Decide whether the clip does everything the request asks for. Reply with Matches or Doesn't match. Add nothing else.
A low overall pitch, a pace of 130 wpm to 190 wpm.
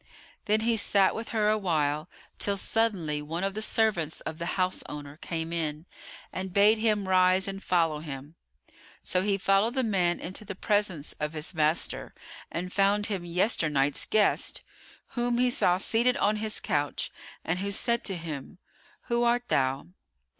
Doesn't match